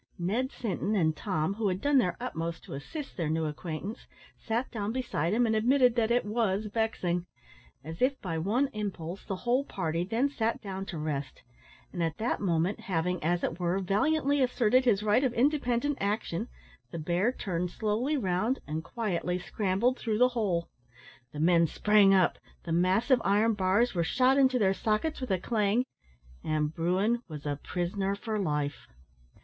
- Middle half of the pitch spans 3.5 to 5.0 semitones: No, wide, 5.5 semitones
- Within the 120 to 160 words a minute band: No, average, 175 wpm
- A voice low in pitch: No, high, 200 Hz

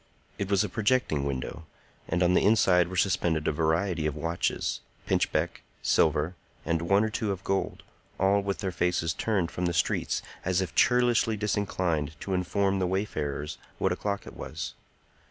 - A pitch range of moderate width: Yes, average, 3.6 semitones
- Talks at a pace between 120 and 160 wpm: No, average, 170 wpm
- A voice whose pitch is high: No, very low, 90 Hz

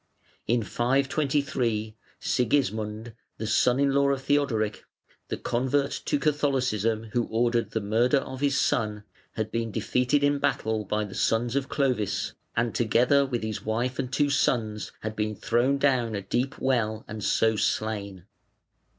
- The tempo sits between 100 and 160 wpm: Yes, average, 150 wpm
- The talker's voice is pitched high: No, low, 120 Hz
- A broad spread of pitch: No, average, 3.9 semitones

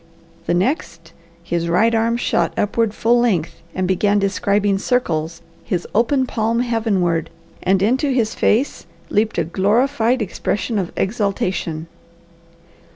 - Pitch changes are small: No, average, 4.4 semitones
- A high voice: Yes, high, 205 Hz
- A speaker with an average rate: No, slow, 125 wpm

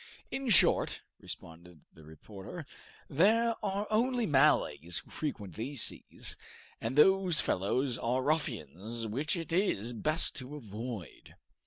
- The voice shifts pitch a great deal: Yes, wide, 8.8 semitones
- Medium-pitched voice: No, low, 130 Hz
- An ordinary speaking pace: No, slow, 125 wpm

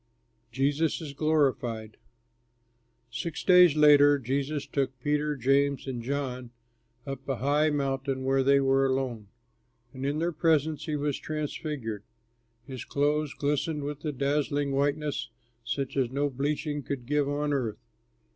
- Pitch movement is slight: Yes, narrow, 1.9 semitones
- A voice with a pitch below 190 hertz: Yes, medium, 140 Hz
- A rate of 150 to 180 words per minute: No, slow, 135 wpm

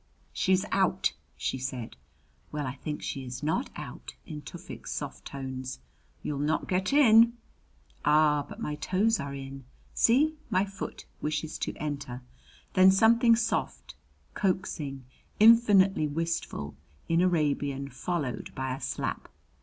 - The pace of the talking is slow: Yes, slow, 130 wpm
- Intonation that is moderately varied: No, wide, 5.9 semitones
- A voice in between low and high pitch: Yes, medium, 155 Hz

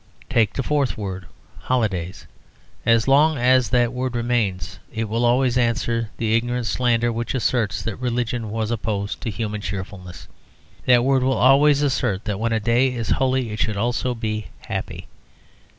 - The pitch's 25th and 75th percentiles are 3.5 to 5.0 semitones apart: No, average, 2.7 semitones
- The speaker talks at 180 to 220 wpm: No, average, 165 wpm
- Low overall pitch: Yes, low, 115 Hz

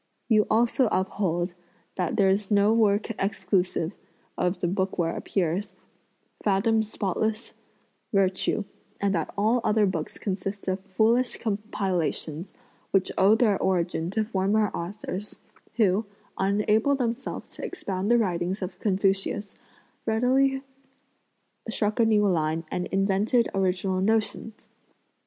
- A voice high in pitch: Yes, high, 200 Hz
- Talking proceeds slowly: Yes, slow, 120 wpm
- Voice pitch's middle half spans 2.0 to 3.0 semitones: Yes, average, 2.7 semitones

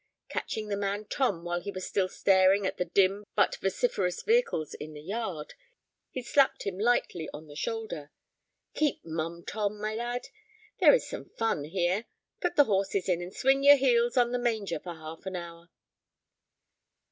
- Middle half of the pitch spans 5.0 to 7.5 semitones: Yes, average, 5.3 semitones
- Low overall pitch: No, high, 195 Hz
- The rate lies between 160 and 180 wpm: Yes, average, 175 wpm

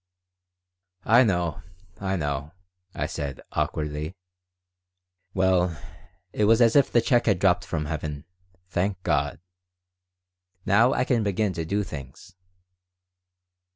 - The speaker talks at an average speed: No, slow, 120 wpm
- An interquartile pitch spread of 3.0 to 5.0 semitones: No, wide, 5.5 semitones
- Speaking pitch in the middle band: No, very low, 90 Hz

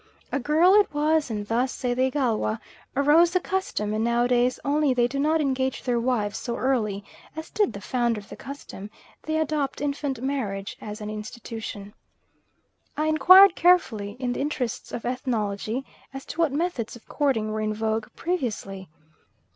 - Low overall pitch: No, very high, 255 Hz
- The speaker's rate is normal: Yes, average, 170 wpm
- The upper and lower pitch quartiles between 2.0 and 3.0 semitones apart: No, average, 5.3 semitones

